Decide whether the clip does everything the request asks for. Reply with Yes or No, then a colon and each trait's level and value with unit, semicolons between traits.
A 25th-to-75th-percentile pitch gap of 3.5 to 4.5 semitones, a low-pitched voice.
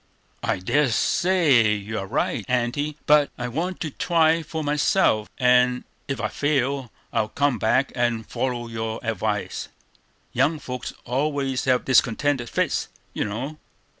Yes: average, 4.0 semitones; low, 130 Hz